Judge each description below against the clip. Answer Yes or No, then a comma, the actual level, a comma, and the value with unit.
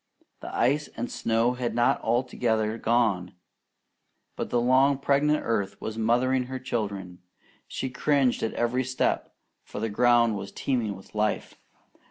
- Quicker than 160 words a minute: No, average, 145 wpm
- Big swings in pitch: No, average, 2.9 semitones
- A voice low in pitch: Yes, low, 120 Hz